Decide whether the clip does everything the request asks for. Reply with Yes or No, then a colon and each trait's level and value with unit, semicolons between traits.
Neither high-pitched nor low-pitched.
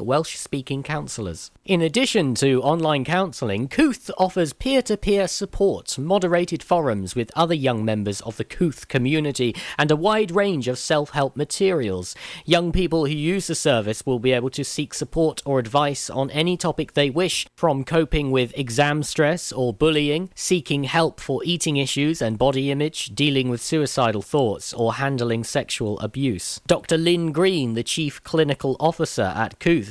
Yes: medium, 145 Hz